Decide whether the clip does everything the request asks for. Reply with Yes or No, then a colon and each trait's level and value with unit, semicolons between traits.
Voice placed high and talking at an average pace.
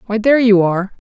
No: high, 215 Hz; fast, 225 wpm